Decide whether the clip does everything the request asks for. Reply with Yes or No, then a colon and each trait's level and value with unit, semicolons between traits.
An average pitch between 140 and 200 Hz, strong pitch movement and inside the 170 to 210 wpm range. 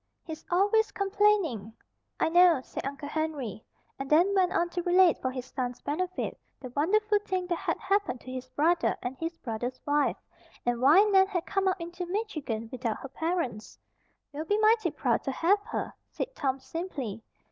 No: very high, 330 Hz; wide, 6.5 semitones; average, 180 wpm